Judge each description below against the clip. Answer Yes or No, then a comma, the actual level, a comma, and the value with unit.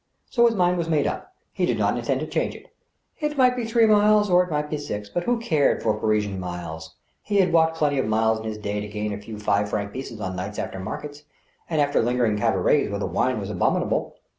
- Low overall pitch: Yes, low, 130 Hz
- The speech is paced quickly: Yes, fast, 245 wpm